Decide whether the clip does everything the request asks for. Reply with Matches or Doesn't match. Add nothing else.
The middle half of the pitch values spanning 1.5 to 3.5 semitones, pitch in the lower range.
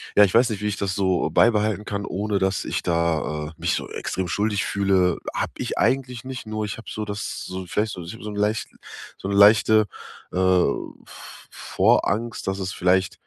Matches